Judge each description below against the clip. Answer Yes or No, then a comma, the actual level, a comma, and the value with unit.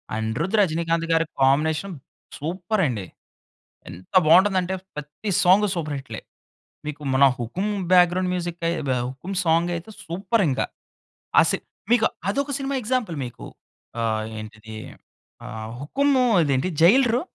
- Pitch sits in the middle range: Yes, medium, 165 Hz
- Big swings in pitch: Yes, wide, 6.2 semitones